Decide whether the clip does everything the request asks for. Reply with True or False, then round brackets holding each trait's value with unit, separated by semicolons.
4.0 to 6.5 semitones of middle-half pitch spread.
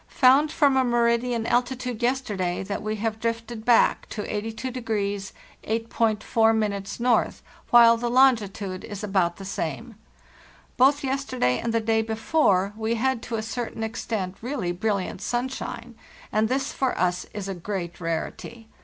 False (3.3 semitones)